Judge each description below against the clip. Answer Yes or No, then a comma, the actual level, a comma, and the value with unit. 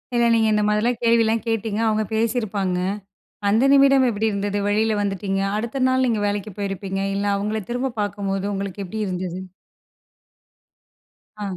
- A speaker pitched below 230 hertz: Yes, high, 210 Hz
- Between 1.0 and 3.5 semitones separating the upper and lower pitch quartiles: Yes, narrow, 2.4 semitones